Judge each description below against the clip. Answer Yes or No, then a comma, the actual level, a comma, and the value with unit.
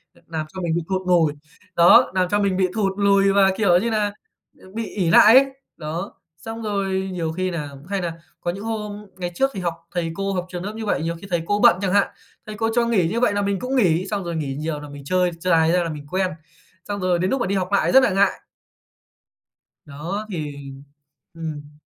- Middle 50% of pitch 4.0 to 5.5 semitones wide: No, average, 3.3 semitones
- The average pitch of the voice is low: No, medium, 185 Hz